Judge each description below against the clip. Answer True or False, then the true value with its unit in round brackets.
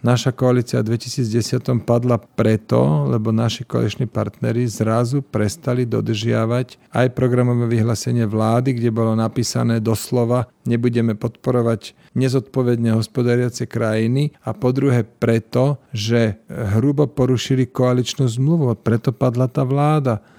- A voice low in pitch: True (120 Hz)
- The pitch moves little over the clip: True (2.0 semitones)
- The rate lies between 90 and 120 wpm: True (115 wpm)